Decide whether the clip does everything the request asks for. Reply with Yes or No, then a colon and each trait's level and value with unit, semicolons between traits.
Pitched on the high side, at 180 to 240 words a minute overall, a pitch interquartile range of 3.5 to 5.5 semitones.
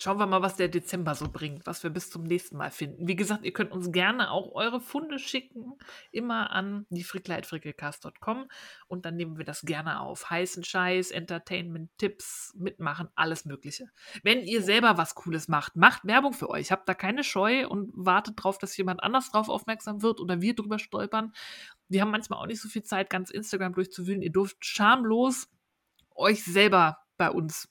Yes: high, 195 Hz; fast, 190 wpm; average, 3.9 semitones